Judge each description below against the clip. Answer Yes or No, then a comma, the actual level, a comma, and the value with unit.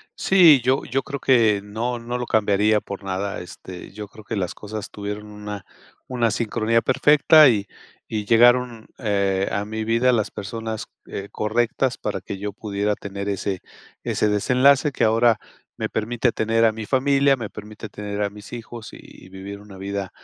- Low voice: Yes, low, 110 Hz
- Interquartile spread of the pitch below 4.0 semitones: Yes, average, 2.9 semitones